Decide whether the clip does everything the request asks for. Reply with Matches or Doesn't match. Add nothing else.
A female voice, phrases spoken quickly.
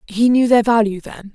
Matches